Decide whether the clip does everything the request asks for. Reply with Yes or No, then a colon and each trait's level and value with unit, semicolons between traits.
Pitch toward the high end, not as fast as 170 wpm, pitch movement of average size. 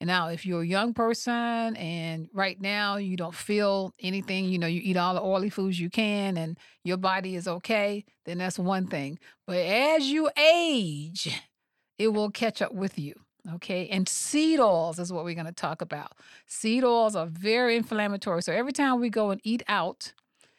No: high, 195 Hz; average, 190 wpm; average, 4.1 semitones